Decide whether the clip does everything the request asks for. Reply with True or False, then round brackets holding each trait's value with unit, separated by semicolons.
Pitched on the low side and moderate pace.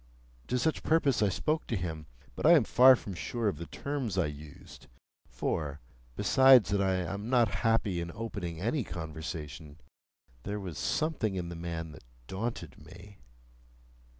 True (95 Hz; 160 wpm)